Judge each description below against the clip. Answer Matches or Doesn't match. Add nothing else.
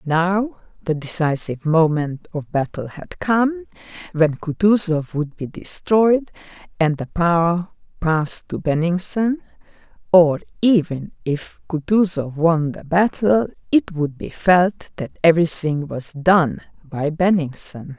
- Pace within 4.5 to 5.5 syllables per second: Doesn't match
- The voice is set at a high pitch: Doesn't match